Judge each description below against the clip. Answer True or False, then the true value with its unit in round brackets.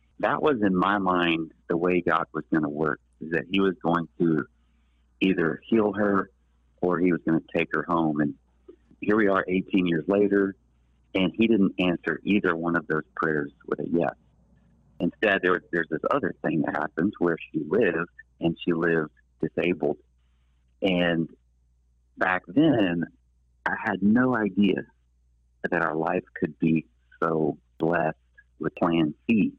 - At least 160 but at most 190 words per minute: True (165 wpm)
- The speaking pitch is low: True (85 Hz)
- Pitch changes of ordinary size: False (6.3 semitones)